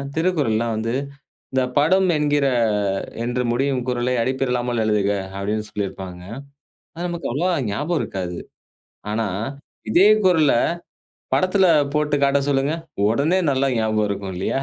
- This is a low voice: Yes, low, 130 Hz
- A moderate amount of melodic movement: No, wide, 5.7 semitones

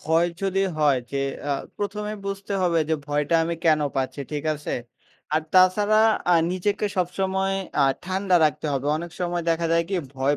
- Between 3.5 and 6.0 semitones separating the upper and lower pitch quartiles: Yes, average, 4.1 semitones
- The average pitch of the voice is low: No, medium, 175 Hz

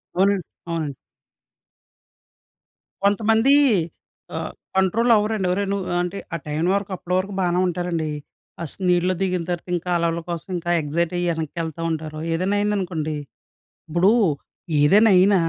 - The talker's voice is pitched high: No, medium, 180 Hz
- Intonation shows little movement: No, average, 3.1 semitones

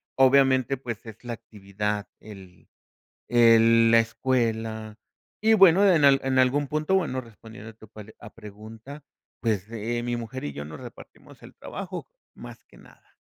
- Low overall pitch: Yes, low, 115 Hz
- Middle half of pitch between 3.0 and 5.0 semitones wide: Yes, average, 3.5 semitones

